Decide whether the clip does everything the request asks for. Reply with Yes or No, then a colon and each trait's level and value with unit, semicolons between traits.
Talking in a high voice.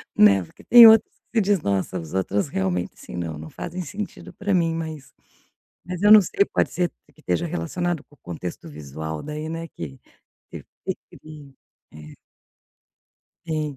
No: medium, 150 Hz